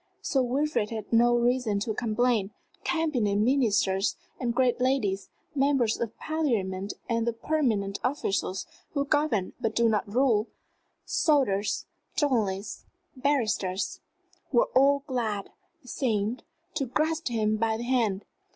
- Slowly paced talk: Yes, slow, 125 wpm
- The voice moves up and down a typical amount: Yes, average, 4.4 semitones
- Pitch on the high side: Yes, high, 235 Hz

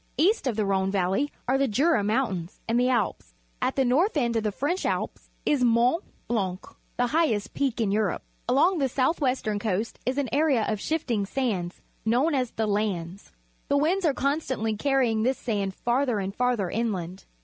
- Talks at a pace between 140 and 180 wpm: No, average, 195 wpm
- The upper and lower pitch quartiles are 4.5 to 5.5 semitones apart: Yes, average, 4.9 semitones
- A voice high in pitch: Yes, high, 235 Hz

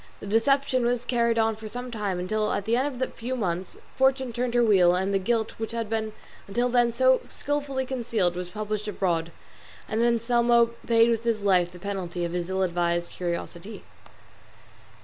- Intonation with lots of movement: No, average, 4.2 semitones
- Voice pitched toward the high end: Yes, high, 225 Hz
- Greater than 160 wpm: Yes, average, 190 wpm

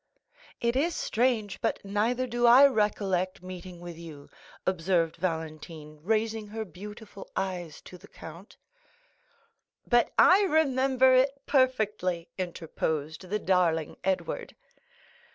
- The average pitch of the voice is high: Yes, high, 195 Hz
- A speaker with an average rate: No, slow, 115 wpm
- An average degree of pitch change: No, wide, 5.7 semitones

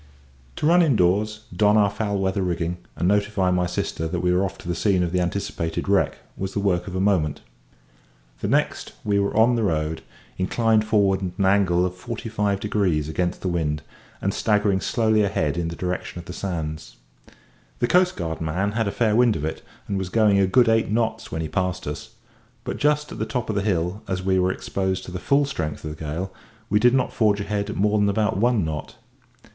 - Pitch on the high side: No, very low, 95 Hz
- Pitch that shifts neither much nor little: Yes, average, 3.3 semitones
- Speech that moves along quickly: Yes, fast, 220 wpm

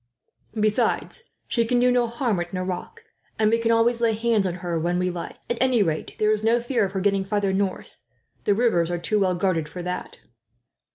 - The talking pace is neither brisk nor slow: No, fast, 215 wpm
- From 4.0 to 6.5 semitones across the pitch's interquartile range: Yes, average, 4.3 semitones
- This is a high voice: Yes, high, 205 Hz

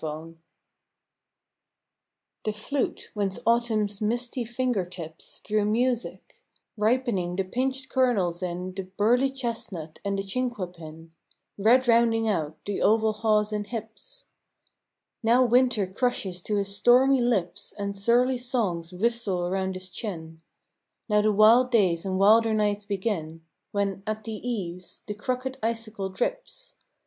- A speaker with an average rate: No, slow, 130 wpm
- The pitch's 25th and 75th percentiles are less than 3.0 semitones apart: No, average, 4.2 semitones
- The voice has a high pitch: Yes, high, 210 Hz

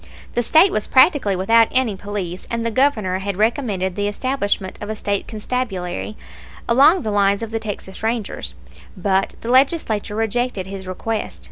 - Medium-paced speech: Yes, average, 160 wpm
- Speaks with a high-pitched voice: Yes, high, 215 Hz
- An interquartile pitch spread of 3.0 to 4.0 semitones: Yes, average, 3.6 semitones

